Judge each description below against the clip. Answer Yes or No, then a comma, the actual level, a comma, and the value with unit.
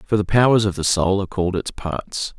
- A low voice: Yes, low, 100 Hz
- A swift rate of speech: Yes, fast, 250 wpm